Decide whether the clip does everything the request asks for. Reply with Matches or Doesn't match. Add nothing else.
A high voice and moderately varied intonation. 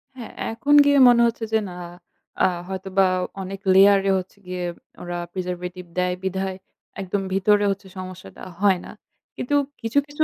Matches